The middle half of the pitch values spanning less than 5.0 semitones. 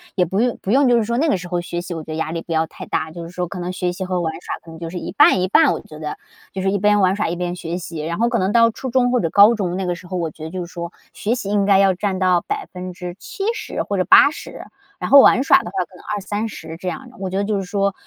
Yes: average, 3.1 semitones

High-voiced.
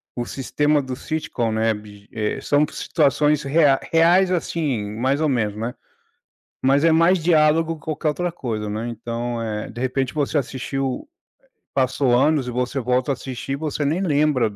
No: low, 135 Hz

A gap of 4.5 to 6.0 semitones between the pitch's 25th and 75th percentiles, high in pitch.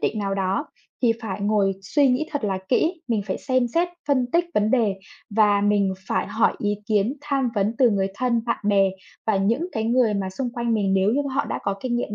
No: average, 4.1 semitones; high, 220 Hz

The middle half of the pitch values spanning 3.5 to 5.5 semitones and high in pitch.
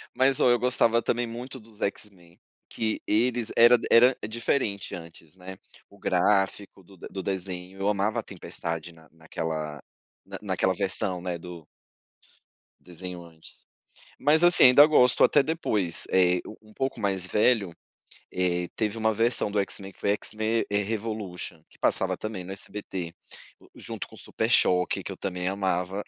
No: average, 4.1 semitones; low, 100 Hz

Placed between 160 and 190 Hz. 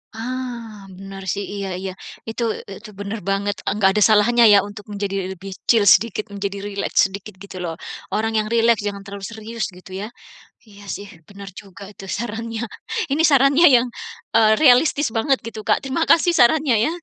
No: high, 215 Hz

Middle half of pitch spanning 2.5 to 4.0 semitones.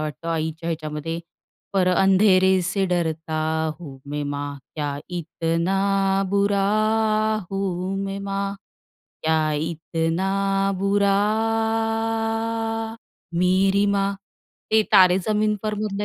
Yes: average, 3.7 semitones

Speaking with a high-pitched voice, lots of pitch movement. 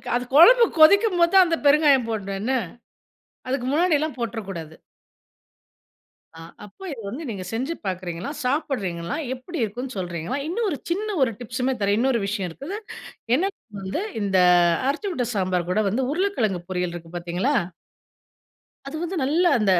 Yes: very high, 250 Hz; wide, 8.5 semitones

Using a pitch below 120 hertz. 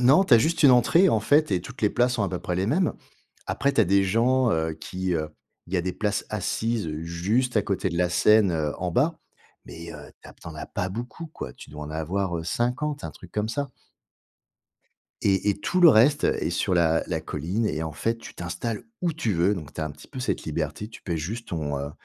Yes: low, 100 Hz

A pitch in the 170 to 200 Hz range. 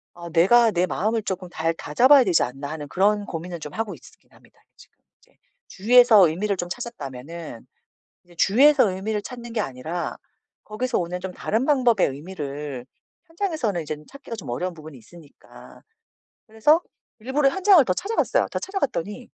Yes: high, 190 Hz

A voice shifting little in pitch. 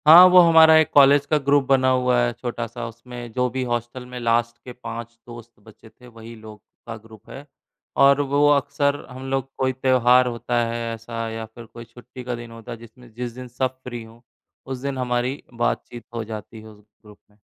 Yes: narrow, 2.1 semitones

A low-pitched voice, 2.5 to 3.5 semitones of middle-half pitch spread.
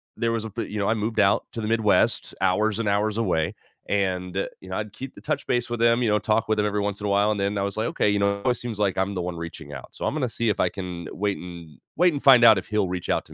Yes: low, 105 Hz; average, 2.9 semitones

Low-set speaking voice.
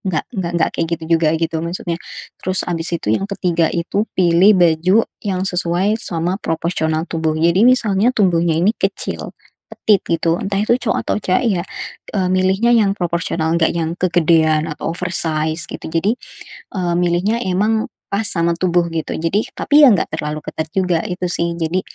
No: medium, 175 Hz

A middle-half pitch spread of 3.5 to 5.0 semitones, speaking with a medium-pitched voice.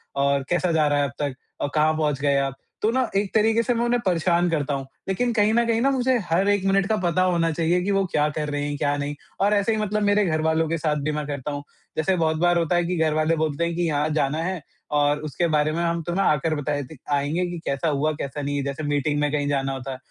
Yes: average, 4.1 semitones; medium, 160 Hz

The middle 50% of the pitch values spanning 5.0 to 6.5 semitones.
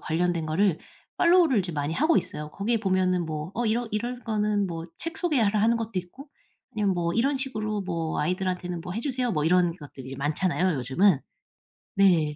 Yes: wide, 5.5 semitones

